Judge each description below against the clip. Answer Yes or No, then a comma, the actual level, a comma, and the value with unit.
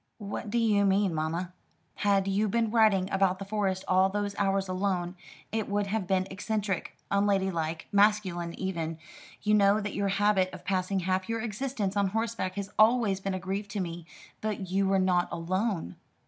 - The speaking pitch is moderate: No, high, 195 Hz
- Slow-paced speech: No, average, 175 wpm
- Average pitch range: No, narrow, 1.9 semitones